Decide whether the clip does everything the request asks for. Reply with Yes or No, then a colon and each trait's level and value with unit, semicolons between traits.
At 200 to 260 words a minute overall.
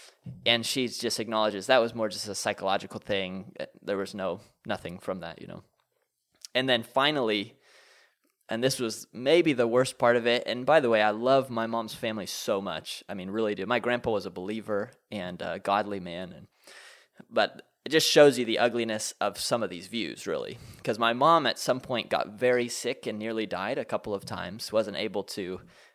Yes: fast, 205 wpm